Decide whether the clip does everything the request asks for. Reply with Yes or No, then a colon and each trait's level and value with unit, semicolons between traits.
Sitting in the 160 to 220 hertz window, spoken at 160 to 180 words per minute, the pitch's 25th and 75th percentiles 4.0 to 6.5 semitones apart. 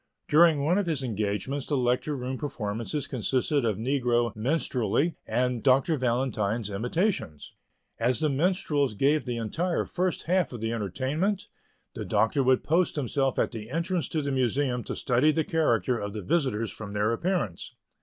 No: low, 130 Hz; average, 165 wpm; average, 5.0 semitones